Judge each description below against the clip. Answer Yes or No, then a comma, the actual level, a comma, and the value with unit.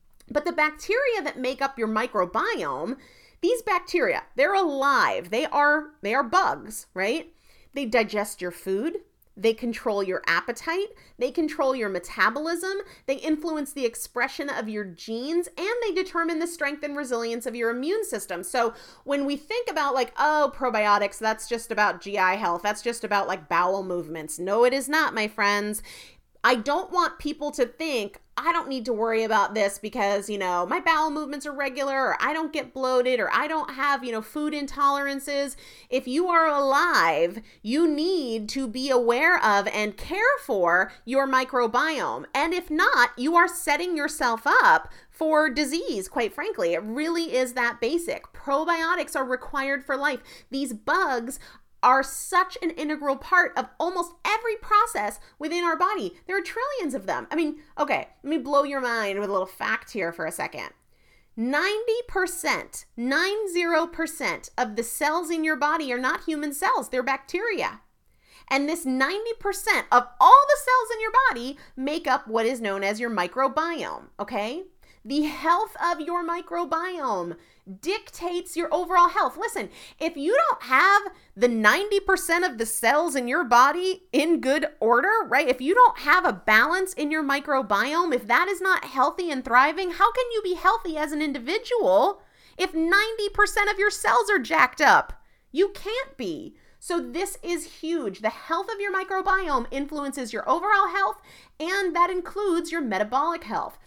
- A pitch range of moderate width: No, wide, 6.4 semitones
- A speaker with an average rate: Yes, average, 170 wpm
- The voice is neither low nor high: No, very high, 295 Hz